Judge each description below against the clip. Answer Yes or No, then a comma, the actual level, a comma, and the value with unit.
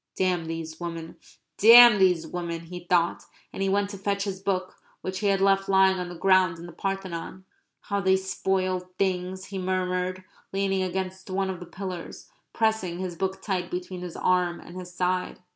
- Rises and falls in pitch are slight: Yes, narrow, 1.4 semitones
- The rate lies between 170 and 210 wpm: Yes, average, 185 wpm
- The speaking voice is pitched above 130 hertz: Yes, medium, 185 Hz